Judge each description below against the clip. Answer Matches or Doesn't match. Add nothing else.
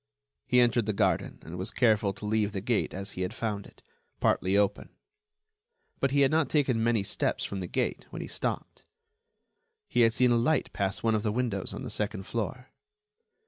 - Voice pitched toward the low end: Matches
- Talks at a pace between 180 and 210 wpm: Matches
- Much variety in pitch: Doesn't match